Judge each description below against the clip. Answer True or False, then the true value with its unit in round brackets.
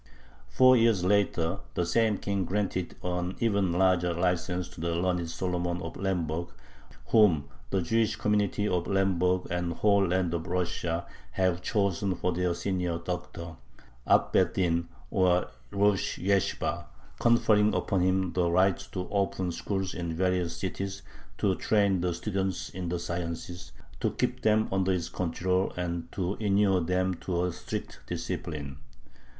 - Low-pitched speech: True (90 Hz)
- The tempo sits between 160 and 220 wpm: False (150 wpm)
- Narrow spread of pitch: True (2.1 semitones)